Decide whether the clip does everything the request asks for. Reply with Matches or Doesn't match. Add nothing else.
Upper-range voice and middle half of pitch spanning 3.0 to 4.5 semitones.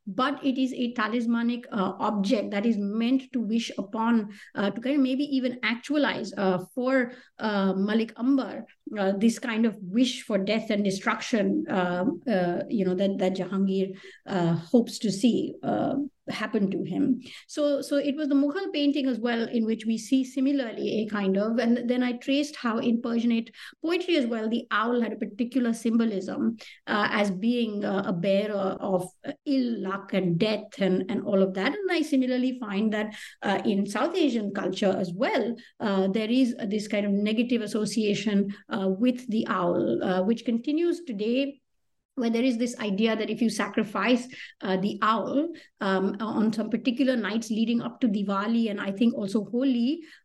Matches